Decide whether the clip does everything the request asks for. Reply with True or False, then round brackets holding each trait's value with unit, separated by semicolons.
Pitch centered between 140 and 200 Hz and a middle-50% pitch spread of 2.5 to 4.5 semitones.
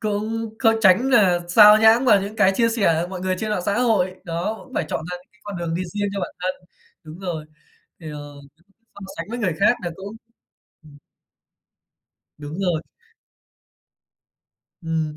True (190 Hz; 4.0 semitones)